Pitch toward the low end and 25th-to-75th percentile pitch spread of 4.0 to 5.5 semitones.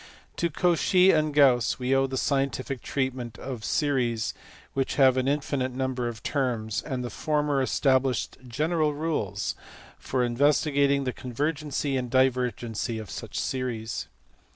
No: low, 130 Hz; average, 2.7 semitones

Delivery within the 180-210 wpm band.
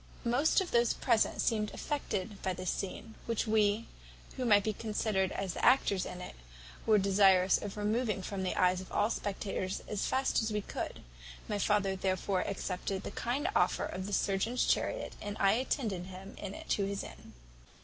Yes: average, 185 wpm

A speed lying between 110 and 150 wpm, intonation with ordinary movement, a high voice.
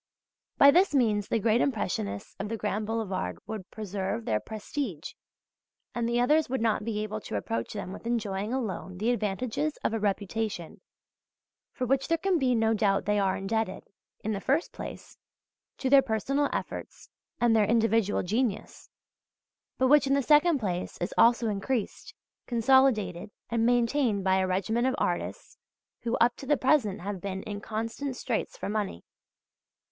No: average, 165 wpm; average, 4.2 semitones; high, 225 Hz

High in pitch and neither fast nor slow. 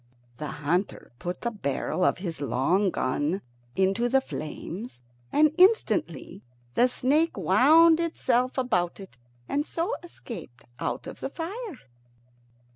No: high, 235 Hz; slow, 125 wpm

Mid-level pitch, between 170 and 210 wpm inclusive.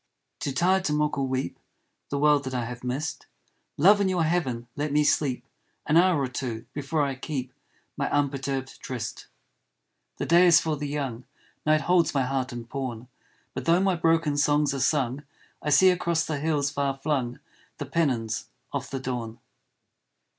Yes: medium, 145 Hz; average, 175 wpm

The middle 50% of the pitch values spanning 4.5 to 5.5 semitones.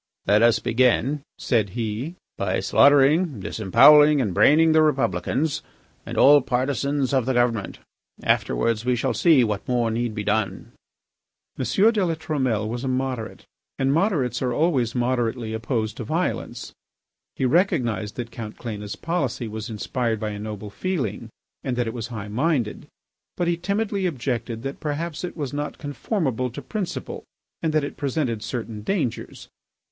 Yes: average, 4.9 semitones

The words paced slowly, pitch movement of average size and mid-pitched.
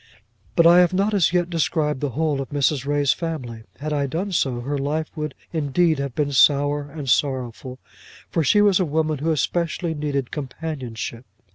No: average, 180 wpm; average, 3.0 semitones; medium, 150 Hz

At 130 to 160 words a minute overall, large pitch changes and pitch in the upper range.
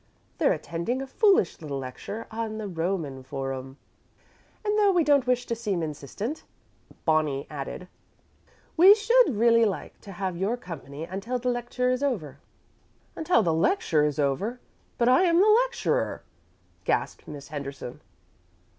Yes: average, 145 wpm; wide, 8.9 semitones; high, 205 Hz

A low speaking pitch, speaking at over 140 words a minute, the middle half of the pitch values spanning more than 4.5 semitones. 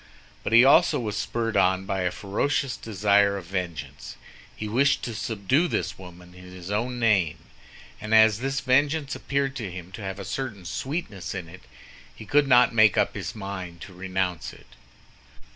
Yes: low, 105 Hz; average, 175 wpm; average, 5.2 semitones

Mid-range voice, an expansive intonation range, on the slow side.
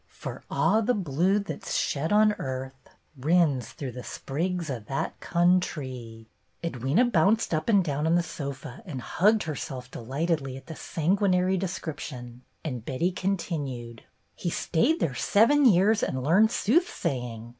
No: medium, 160 Hz; wide, 6.2 semitones; average, 150 wpm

